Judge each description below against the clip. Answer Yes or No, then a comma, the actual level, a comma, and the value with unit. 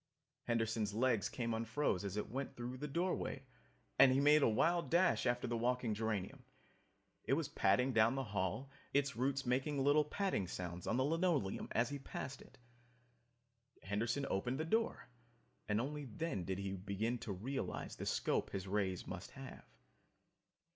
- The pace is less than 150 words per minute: No, average, 165 wpm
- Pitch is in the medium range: No, low, 120 Hz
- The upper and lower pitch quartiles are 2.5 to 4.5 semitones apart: No, average, 5.0 semitones